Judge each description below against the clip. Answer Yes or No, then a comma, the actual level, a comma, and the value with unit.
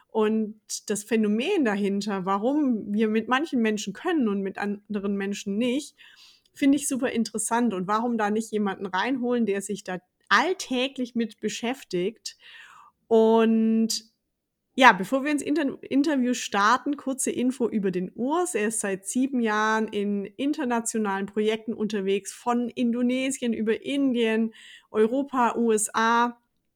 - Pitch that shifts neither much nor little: Yes, average, 3.3 semitones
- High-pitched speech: Yes, high, 225 Hz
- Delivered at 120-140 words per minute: Yes, average, 130 wpm